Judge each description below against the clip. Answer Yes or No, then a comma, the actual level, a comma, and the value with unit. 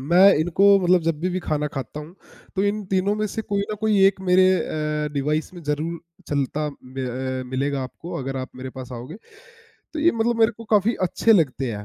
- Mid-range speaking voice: Yes, medium, 165 Hz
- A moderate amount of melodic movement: No, wide, 6.5 semitones